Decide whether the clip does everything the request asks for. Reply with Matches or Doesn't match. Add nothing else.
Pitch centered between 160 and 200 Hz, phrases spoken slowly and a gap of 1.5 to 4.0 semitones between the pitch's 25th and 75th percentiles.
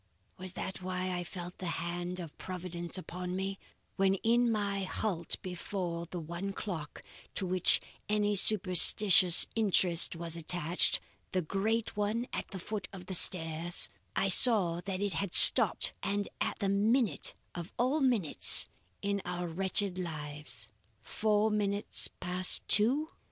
Doesn't match